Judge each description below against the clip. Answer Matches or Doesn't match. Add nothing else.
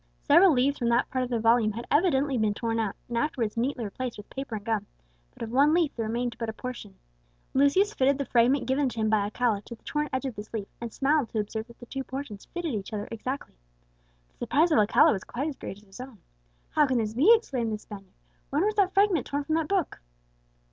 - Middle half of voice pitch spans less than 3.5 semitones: Doesn't match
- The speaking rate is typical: Doesn't match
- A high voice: Matches